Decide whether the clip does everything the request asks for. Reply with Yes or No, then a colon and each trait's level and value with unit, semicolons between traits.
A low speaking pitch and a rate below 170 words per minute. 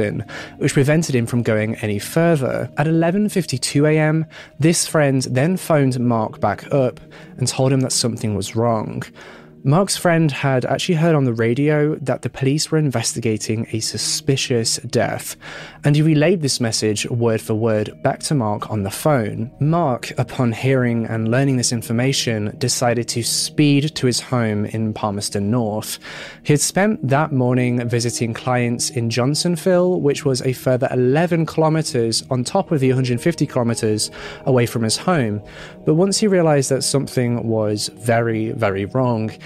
Yes: low, 125 Hz; average, 160 wpm